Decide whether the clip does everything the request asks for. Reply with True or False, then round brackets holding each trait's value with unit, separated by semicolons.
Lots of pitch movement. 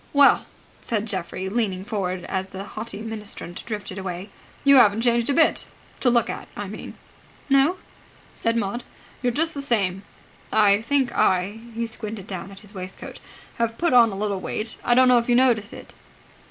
False (3.7 semitones)